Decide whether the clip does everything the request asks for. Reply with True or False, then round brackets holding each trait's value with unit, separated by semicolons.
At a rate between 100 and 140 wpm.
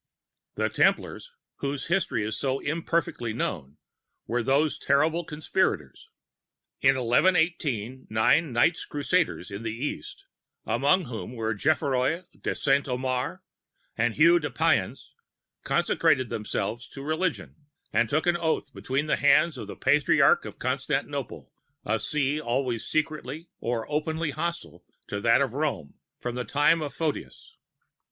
True (135 wpm)